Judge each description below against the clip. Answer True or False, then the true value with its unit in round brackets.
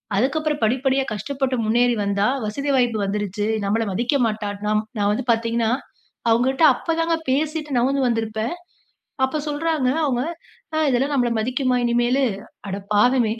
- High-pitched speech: True (245 Hz)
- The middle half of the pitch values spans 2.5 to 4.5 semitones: True (4.0 semitones)